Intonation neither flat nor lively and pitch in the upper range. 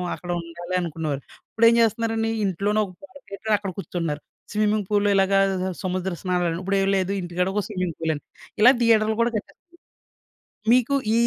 Yes: average, 3.5 semitones; high, 195 Hz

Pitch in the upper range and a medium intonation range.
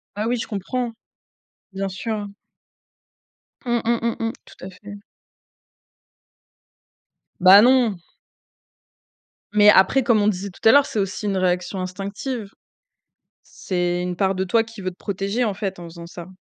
Yes: high, 200 Hz; average, 3.3 semitones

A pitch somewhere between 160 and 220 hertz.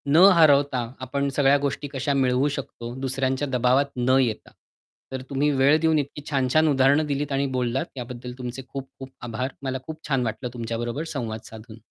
No: low, 135 Hz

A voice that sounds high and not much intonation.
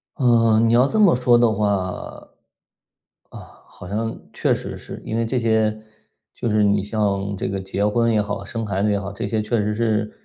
No: low, 110 Hz; narrow, 2.2 semitones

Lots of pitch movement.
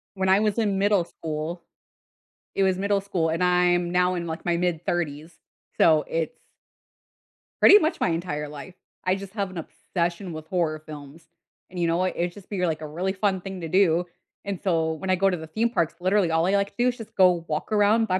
No: average, 2.9 semitones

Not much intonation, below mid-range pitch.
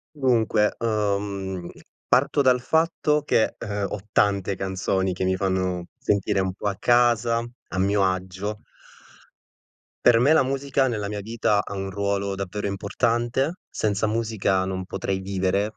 No: average, 3.5 semitones; low, 100 Hz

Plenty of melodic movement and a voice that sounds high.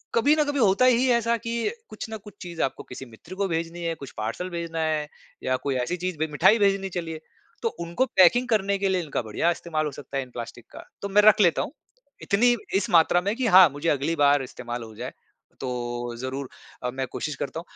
No: wide, 6.5 semitones; medium, 170 Hz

